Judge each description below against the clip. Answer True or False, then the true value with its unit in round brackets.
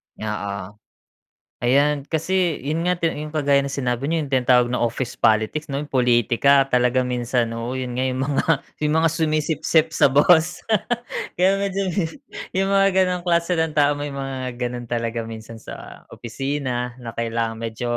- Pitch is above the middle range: False (135 Hz)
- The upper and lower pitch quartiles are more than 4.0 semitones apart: True (4.5 semitones)